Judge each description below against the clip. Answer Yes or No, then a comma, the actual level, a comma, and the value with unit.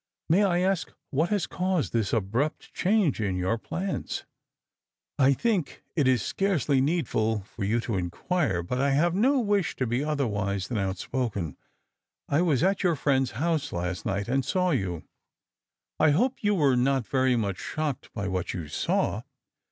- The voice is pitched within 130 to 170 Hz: Yes, low, 135 Hz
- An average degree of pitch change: No, wide, 8.8 semitones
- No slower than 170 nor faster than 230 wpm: Yes, average, 180 wpm